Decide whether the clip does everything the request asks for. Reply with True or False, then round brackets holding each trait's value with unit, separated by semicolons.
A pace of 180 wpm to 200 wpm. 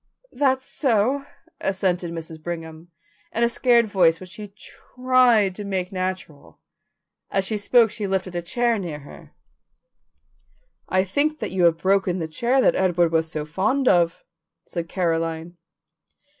False (145 wpm)